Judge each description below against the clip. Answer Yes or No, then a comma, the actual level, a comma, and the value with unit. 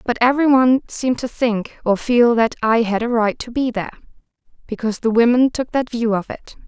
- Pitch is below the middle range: No, high, 235 Hz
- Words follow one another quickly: Yes, fast, 215 wpm